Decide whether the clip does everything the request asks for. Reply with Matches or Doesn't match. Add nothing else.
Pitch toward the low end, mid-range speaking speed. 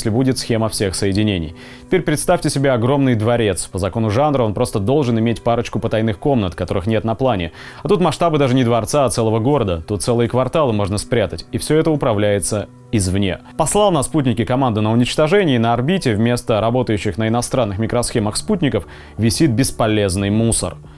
Doesn't match